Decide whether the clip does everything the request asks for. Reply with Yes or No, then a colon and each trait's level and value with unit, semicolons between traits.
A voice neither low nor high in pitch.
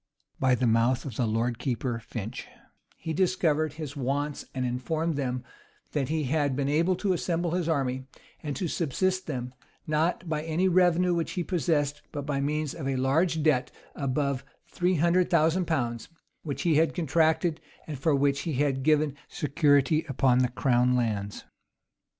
Yes: medium, 145 Hz